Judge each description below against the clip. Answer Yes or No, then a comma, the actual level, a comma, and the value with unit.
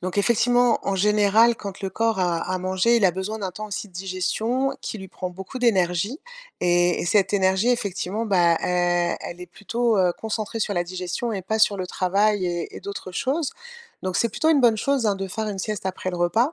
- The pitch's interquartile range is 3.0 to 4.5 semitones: Yes, average, 3.5 semitones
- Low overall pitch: No, high, 200 Hz